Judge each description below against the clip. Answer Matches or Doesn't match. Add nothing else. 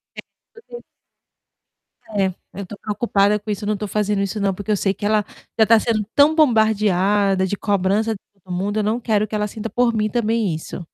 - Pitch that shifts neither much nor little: Doesn't match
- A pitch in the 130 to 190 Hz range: Doesn't match